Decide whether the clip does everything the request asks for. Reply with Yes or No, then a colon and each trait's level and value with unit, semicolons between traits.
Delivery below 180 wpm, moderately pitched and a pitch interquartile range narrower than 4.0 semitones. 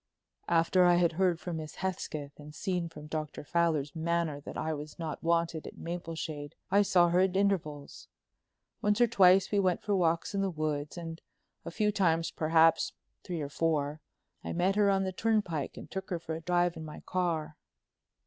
No: average, 190 wpm; medium, 170 Hz; average, 2.9 semitones